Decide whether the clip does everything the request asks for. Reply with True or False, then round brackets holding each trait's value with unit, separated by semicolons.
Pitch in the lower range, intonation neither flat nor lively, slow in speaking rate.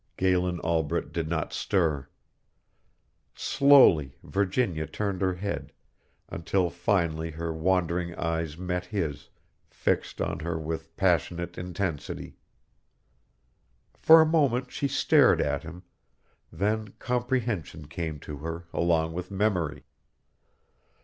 True (85 Hz; 3.7 semitones; 110 wpm)